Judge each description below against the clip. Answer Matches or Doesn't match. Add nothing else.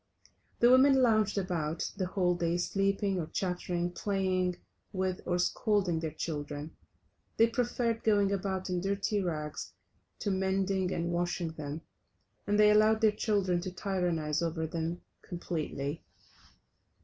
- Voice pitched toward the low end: Doesn't match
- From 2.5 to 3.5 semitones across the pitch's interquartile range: Matches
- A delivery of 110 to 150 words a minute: Matches